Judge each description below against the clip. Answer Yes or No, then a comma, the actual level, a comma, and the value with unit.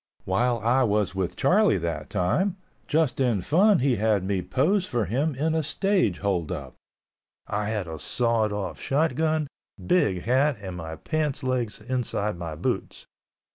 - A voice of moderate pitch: No, low, 115 Hz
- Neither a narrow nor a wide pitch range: No, wide, 7.9 semitones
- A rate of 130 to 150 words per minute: No, average, 165 wpm